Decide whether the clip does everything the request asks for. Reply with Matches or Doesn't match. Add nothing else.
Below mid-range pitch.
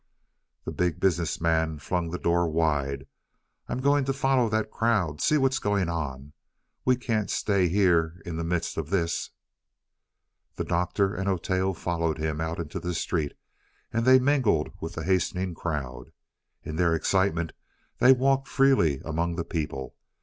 Matches